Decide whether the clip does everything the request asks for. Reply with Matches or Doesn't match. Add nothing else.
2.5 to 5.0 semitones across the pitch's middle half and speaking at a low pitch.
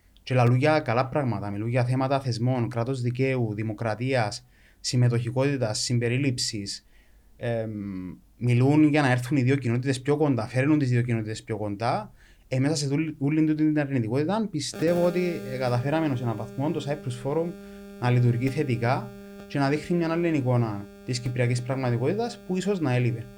Matches